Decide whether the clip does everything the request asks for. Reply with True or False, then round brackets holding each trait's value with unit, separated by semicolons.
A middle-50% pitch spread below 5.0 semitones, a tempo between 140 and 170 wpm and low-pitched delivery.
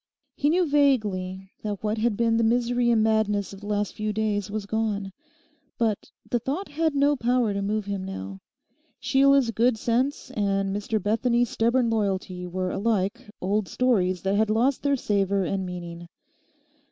False (3.5 semitones; 165 wpm; 215 Hz)